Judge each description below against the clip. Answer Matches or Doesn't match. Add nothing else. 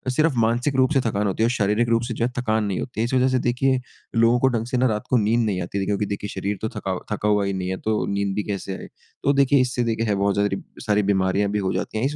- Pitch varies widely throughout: Doesn't match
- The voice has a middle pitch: Doesn't match